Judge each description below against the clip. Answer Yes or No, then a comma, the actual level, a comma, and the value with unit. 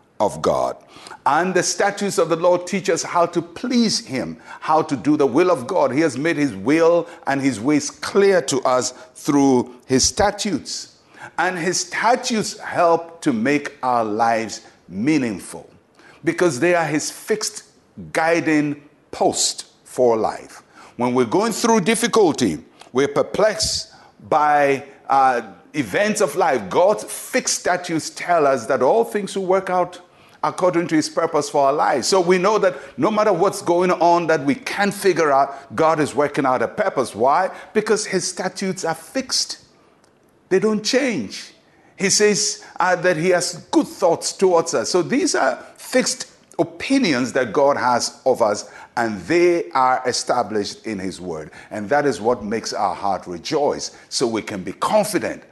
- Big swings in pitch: Yes, wide, 6.0 semitones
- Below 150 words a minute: No, average, 165 wpm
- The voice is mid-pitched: Yes, medium, 170 Hz